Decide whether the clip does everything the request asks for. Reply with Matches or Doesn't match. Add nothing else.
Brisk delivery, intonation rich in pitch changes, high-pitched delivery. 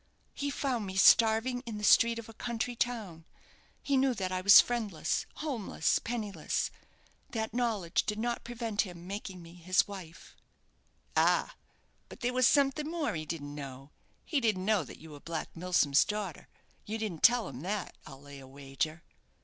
Doesn't match